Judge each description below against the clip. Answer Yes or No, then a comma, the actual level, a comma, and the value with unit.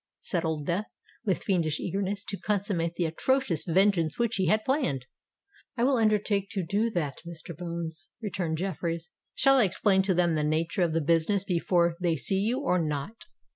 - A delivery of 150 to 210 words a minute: Yes, average, 180 wpm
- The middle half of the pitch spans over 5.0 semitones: No, average, 3.8 semitones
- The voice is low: No, medium, 180 Hz